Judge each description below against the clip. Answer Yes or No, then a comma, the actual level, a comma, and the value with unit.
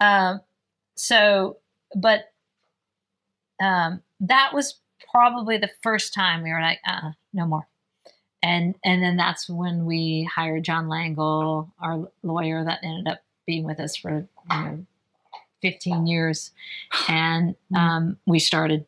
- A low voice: No, medium, 170 Hz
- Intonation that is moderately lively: Yes, average, 3.2 semitones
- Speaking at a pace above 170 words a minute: No, slow, 135 wpm